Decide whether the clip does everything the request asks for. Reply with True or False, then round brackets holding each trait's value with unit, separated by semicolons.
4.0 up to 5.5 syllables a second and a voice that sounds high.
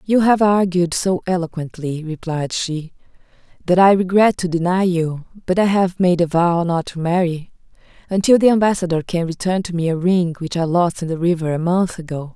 False (5.2 syllables/s; 175 Hz)